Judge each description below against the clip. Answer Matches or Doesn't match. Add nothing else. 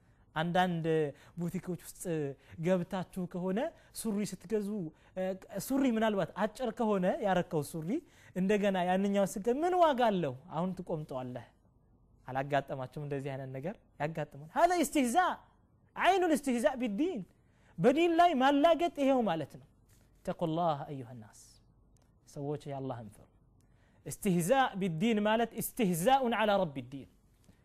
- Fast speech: Matches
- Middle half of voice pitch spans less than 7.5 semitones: Doesn't match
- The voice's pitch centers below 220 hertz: Matches